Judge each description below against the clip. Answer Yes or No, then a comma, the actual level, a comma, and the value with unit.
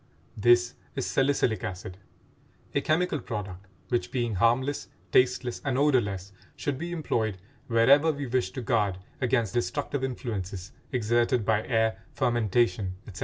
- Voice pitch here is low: Yes, low, 120 Hz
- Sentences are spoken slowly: Yes, slow, 130 wpm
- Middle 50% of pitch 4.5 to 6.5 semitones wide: No, average, 4.0 semitones